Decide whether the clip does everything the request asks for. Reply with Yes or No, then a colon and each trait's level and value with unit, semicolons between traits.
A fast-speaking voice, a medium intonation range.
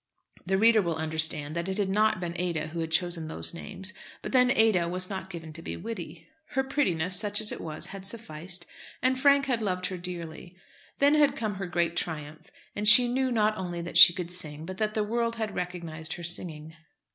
Yes: fast, 215 wpm; average, 4.6 semitones